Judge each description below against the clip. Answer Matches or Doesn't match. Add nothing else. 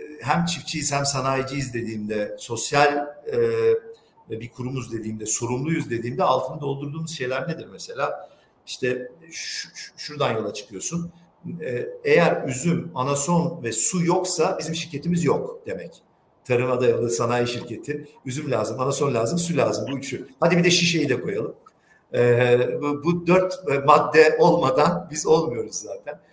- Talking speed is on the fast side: Doesn't match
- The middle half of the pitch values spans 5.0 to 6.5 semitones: Matches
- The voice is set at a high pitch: Doesn't match